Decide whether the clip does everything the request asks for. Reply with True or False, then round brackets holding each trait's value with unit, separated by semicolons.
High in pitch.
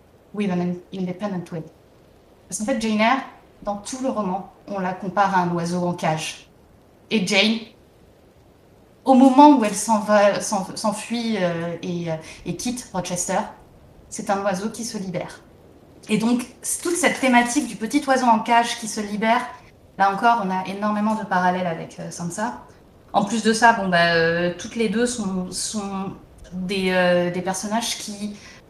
True (205 Hz)